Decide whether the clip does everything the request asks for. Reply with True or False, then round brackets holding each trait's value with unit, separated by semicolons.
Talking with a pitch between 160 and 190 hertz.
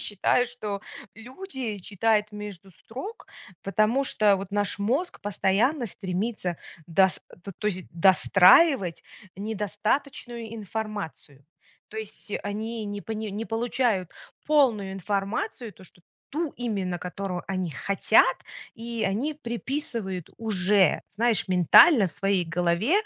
False (210 Hz)